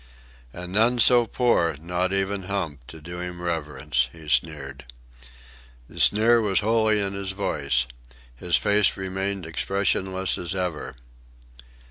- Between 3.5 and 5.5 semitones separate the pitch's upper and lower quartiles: Yes, average, 3.8 semitones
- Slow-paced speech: Yes, slow, 130 wpm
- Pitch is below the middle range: Yes, very low, 95 Hz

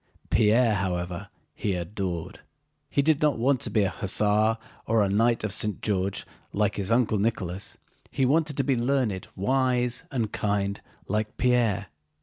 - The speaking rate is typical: Yes, average, 155 wpm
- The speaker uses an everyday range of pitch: Yes, average, 3.8 semitones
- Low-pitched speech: Yes, low, 110 Hz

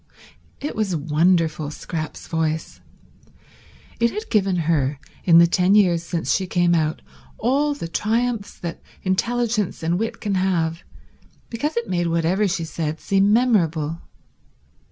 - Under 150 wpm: Yes, slow, 135 wpm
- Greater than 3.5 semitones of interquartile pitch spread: Yes, average, 4.5 semitones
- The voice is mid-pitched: Yes, medium, 180 Hz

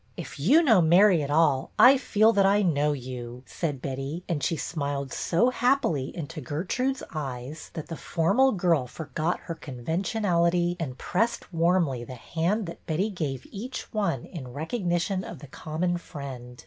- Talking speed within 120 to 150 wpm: No, average, 165 wpm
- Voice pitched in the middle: Yes, medium, 165 Hz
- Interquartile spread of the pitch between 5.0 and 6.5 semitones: Yes, average, 5.3 semitones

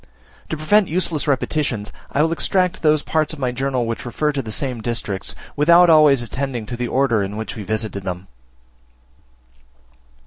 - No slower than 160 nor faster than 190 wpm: Yes, average, 170 wpm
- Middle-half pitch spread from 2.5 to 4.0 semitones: No, average, 5.2 semitones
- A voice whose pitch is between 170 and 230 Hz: No, low, 135 Hz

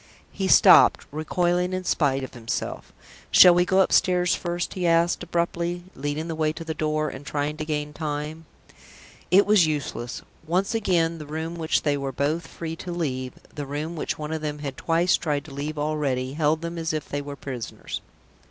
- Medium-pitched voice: Yes, medium, 155 Hz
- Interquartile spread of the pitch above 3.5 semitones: No, average, 2.8 semitones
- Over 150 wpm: Yes, average, 190 wpm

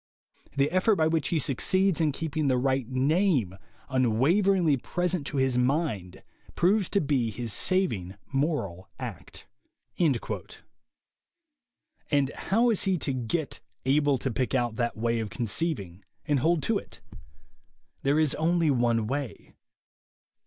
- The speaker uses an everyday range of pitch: No, wide, 5.8 semitones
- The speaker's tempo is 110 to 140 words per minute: Yes, slow, 135 wpm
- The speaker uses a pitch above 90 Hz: Yes, medium, 140 Hz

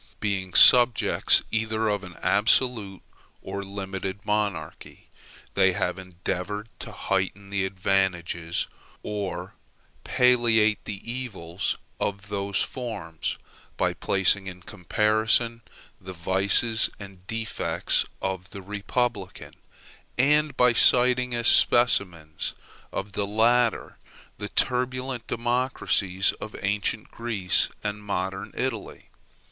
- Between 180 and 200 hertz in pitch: No, low, 105 Hz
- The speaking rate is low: Yes, slow, 105 wpm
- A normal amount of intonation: Yes, average, 3.6 semitones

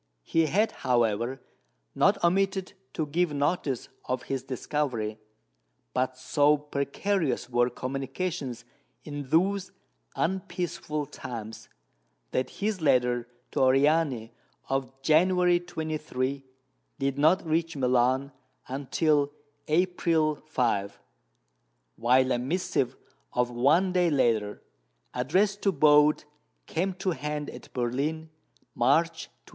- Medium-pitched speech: Yes, medium, 145 Hz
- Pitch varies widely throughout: No, average, 4.6 semitones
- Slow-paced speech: Yes, slow, 105 wpm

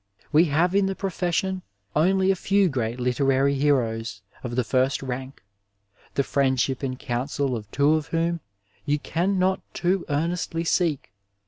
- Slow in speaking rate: No, average, 150 wpm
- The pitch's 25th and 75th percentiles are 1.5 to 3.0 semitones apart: No, average, 5.2 semitones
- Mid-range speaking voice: Yes, medium, 145 Hz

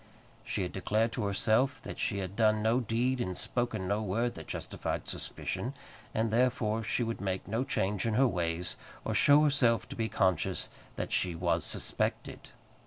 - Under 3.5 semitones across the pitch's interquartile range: No, average, 4.1 semitones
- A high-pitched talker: No, low, 110 Hz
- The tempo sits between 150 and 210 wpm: Yes, average, 175 wpm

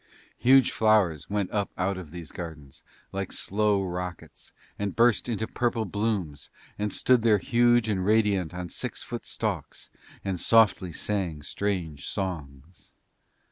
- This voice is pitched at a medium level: No, low, 100 Hz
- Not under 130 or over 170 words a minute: Yes, average, 140 wpm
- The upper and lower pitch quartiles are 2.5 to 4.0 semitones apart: Yes, average, 3.7 semitones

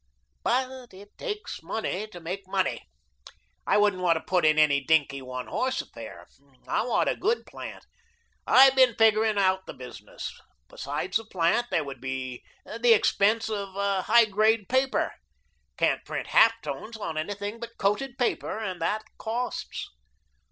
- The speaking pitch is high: Yes, high, 205 Hz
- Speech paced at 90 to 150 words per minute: No, average, 160 wpm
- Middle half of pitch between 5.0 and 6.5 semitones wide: Yes, average, 5.3 semitones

